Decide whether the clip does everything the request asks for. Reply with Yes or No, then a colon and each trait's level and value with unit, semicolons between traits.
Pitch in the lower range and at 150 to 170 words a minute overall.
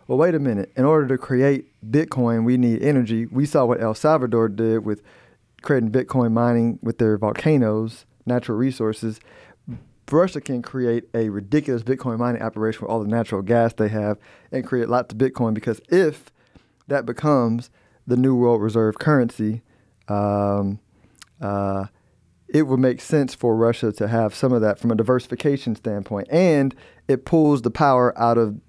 Yes: low, 120 Hz; average, 165 wpm